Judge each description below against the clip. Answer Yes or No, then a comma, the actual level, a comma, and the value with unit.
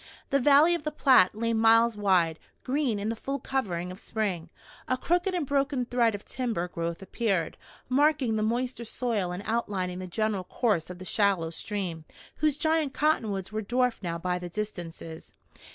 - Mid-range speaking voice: No, high, 220 Hz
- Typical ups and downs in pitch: No, wide, 5.8 semitones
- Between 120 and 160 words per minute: No, average, 175 wpm